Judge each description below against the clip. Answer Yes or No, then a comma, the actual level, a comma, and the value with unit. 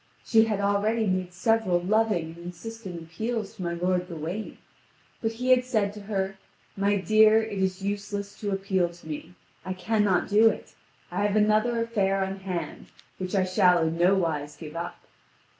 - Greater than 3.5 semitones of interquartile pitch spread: No, average, 3.2 semitones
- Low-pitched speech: No, high, 195 Hz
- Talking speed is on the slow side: No, average, 175 wpm